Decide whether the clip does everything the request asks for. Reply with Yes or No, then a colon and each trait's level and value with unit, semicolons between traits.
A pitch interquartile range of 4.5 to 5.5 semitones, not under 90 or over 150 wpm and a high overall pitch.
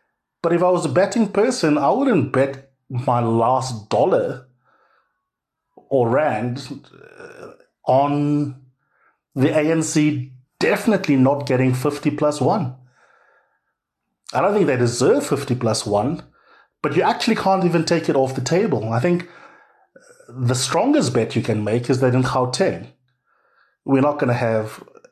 No: average, 5.1 semitones; average, 145 wpm; medium, 140 Hz